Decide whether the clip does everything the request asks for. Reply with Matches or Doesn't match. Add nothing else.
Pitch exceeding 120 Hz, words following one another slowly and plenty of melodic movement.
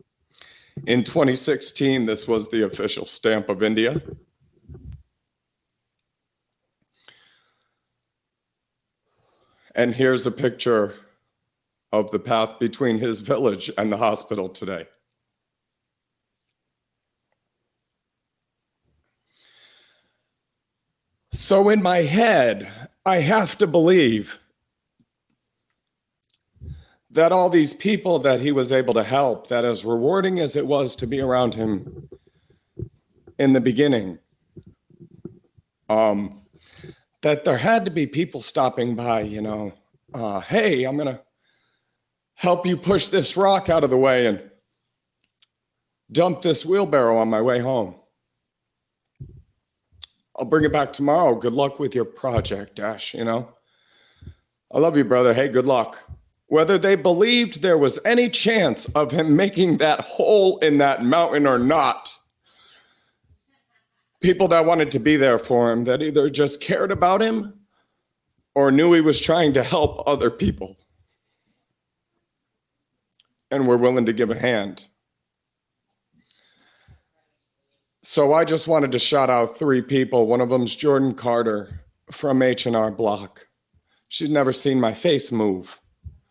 Matches